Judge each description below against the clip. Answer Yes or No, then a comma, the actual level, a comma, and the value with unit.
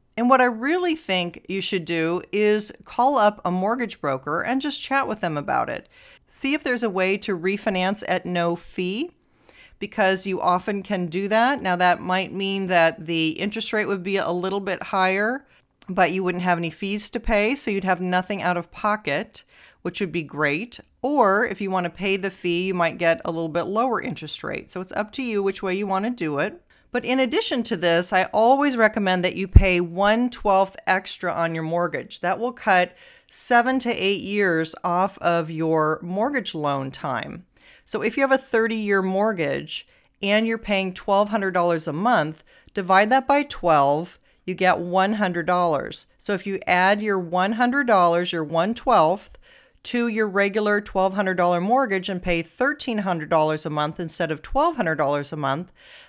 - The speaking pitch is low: No, high, 195 Hz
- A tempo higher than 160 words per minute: Yes, average, 185 wpm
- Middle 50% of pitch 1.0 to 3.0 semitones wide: No, average, 4.0 semitones